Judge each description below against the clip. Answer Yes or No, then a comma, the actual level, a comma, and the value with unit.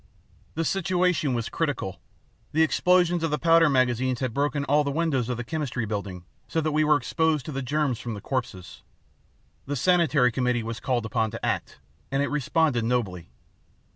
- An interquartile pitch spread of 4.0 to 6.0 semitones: Yes, average, 4.7 semitones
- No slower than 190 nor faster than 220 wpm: No, average, 180 wpm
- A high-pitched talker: No, low, 135 Hz